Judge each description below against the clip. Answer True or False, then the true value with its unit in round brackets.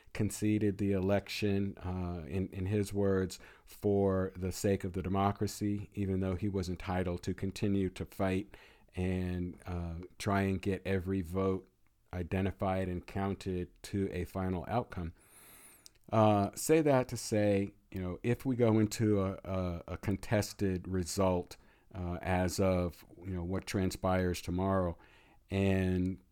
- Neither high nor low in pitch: False (95 Hz)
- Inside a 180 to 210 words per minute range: False (140 wpm)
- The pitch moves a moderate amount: False (1.8 semitones)